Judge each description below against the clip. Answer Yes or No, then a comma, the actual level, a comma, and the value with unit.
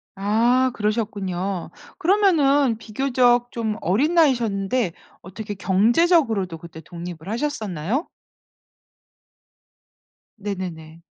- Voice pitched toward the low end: No, high, 215 Hz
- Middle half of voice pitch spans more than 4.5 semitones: Yes, wide, 5.4 semitones